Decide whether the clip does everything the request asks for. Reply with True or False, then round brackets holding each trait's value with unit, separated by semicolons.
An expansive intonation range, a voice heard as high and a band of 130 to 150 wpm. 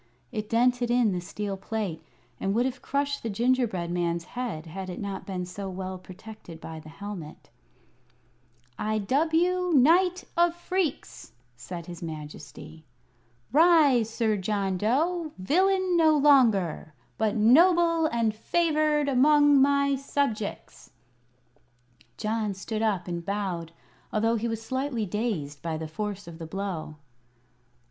True (7.4 semitones; 220 Hz; 135 wpm)